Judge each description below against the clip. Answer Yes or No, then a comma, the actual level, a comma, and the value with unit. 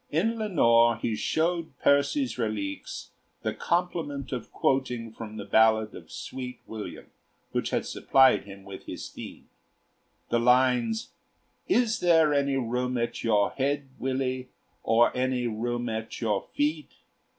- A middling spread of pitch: Yes, average, 4.1 semitones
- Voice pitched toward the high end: No, low, 125 Hz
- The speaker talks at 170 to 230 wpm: No, slow, 135 wpm